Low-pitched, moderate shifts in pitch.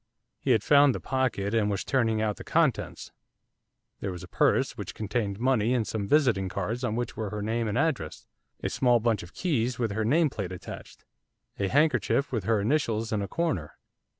Yes: low, 115 Hz; average, 4.0 semitones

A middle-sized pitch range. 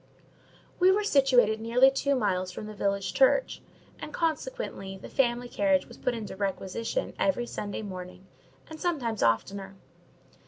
No: wide, 6.3 semitones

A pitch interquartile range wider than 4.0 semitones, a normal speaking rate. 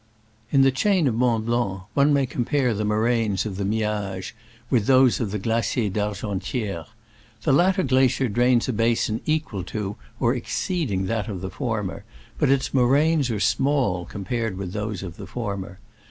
Yes: average, 4.4 semitones; average, 170 wpm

